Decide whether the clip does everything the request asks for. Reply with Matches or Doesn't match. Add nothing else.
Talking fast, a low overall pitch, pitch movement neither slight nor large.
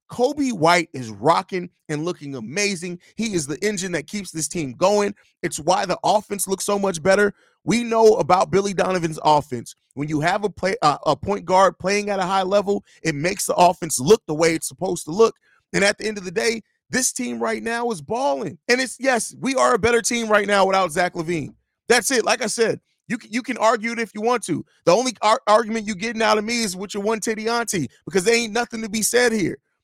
Doesn't match